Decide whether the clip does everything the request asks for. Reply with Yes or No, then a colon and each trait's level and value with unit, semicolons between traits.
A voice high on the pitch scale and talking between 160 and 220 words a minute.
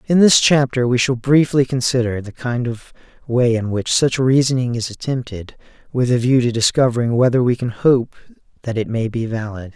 No: low, 125 Hz; average, 190 wpm